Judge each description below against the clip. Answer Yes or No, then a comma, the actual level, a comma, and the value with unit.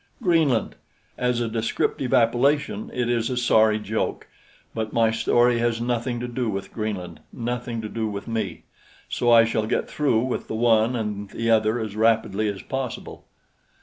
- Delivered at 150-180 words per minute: Yes, average, 170 wpm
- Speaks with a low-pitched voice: Yes, low, 115 Hz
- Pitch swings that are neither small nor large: No, narrow, 1.9 semitones